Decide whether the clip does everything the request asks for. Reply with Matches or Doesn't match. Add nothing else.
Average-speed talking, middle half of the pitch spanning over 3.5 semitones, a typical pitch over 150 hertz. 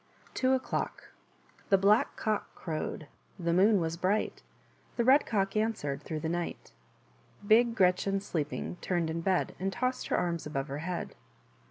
Matches